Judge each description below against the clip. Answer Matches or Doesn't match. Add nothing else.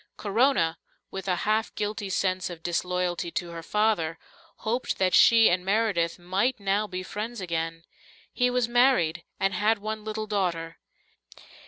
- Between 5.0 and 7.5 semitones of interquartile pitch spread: Doesn't match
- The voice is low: Doesn't match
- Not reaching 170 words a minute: Matches